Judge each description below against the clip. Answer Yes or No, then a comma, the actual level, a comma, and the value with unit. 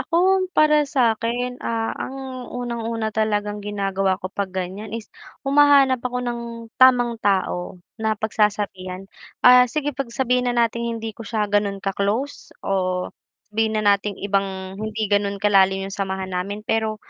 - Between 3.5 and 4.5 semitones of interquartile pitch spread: Yes, average, 3.9 semitones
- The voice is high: Yes, high, 220 Hz